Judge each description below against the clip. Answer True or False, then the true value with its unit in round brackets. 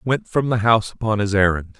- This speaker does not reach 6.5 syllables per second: False (6.6 syllables/s)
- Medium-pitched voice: False (110 Hz)